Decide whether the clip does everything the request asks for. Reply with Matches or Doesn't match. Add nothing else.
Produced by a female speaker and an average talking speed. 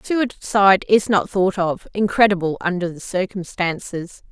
Doesn't match